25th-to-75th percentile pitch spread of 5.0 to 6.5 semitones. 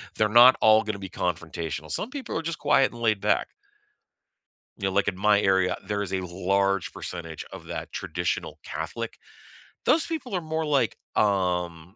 Yes: wide, 5.5 semitones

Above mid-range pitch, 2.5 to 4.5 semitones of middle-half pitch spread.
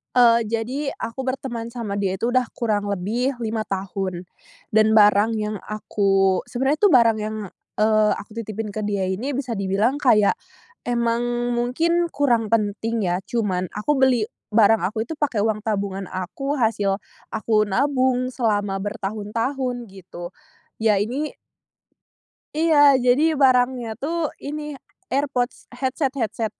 Yes: high, 225 Hz; average, 3.7 semitones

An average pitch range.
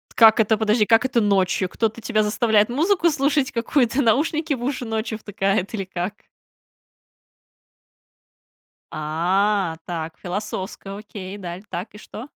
Yes: average, 3.7 semitones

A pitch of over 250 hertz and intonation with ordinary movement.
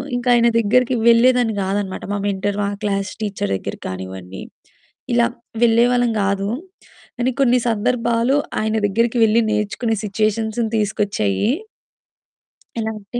No: high, 220 Hz; average, 3.0 semitones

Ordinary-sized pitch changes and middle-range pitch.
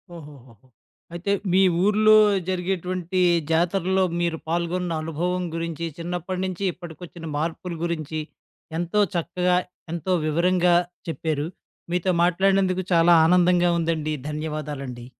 No: narrow, 2.1 semitones; medium, 175 Hz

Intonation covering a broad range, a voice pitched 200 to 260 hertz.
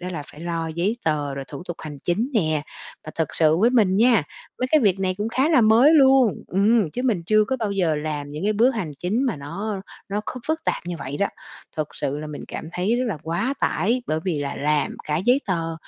No: wide, 6.5 semitones; medium, 185 Hz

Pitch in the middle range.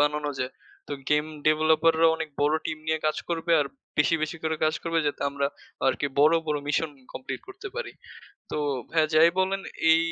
Yes: medium, 155 Hz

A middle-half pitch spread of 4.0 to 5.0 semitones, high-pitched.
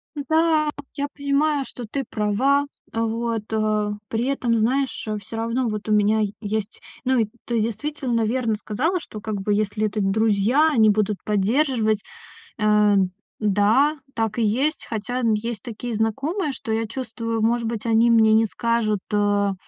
No: average, 3.3 semitones; high, 225 Hz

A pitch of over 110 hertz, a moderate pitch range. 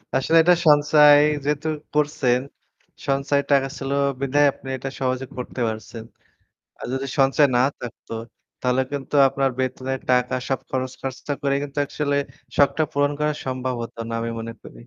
No: low, 135 Hz; narrow, 2.0 semitones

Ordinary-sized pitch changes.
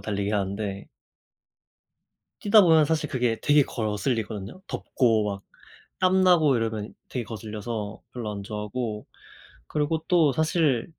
No: wide, 6.5 semitones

